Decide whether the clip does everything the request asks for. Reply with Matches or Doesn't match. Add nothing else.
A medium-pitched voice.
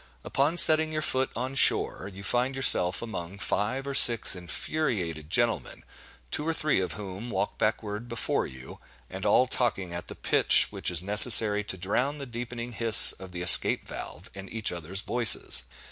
Doesn't match